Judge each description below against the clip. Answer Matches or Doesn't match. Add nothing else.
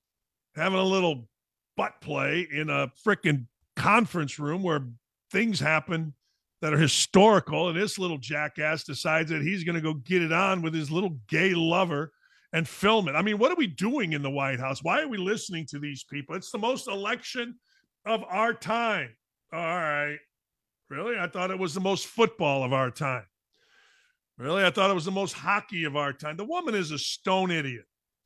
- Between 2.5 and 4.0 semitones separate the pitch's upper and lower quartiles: Doesn't match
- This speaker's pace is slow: Doesn't match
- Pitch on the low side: Doesn't match